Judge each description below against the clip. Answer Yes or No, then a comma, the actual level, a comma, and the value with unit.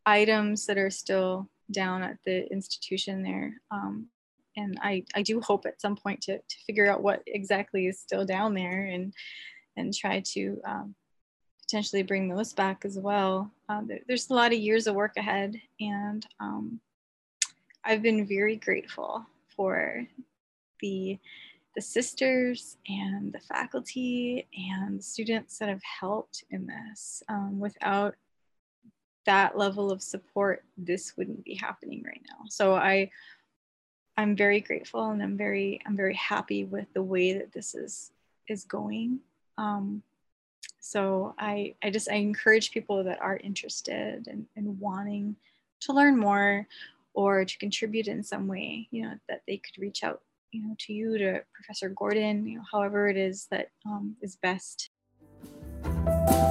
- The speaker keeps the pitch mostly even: Yes, narrow, 2.1 semitones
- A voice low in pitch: No, high, 205 Hz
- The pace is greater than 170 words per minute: No, average, 155 wpm